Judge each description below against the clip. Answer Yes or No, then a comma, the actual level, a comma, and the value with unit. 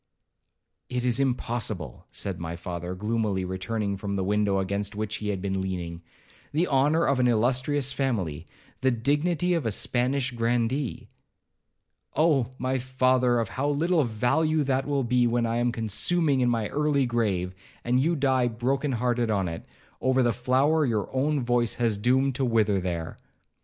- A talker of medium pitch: No, low, 120 Hz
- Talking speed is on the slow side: No, average, 160 wpm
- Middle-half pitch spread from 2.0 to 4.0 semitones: No, average, 4.4 semitones